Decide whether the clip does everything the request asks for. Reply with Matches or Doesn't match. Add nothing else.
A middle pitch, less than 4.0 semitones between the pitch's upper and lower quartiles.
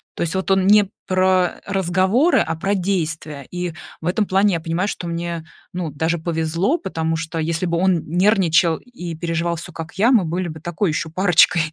Matches